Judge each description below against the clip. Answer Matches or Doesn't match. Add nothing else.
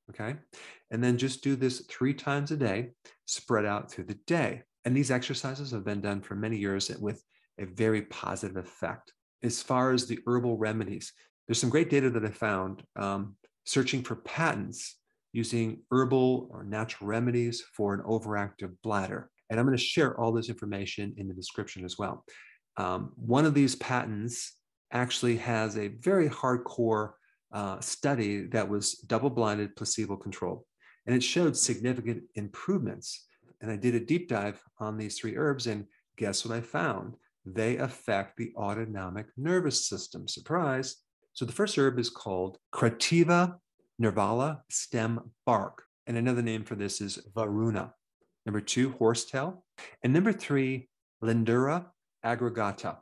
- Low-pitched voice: Matches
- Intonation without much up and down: Doesn't match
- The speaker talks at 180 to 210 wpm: Doesn't match